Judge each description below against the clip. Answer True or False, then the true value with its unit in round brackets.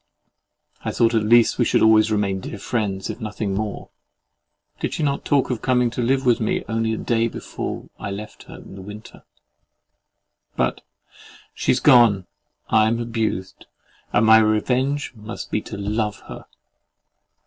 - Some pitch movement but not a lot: False (2.2 semitones)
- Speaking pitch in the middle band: False (110 Hz)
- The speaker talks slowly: False (160 wpm)